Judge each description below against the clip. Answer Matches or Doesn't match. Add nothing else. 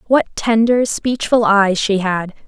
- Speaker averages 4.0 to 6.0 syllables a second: Doesn't match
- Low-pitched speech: Doesn't match